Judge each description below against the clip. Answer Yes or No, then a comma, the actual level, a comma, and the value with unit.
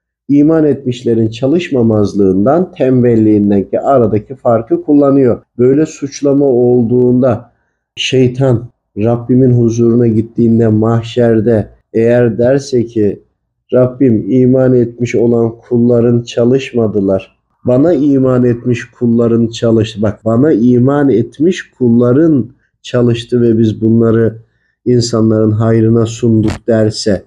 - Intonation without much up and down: Yes, narrow, 2.0 semitones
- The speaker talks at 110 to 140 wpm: No, slow, 95 wpm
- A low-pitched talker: Yes, low, 120 Hz